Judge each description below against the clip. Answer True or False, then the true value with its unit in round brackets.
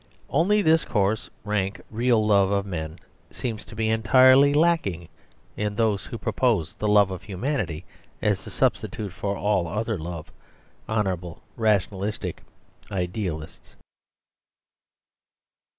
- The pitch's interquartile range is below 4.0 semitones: True (3.2 semitones)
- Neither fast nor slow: False (120 wpm)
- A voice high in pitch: False (105 Hz)